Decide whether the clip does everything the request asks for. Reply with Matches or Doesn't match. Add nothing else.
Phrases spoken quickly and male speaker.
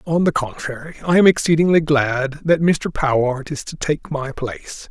Doesn't match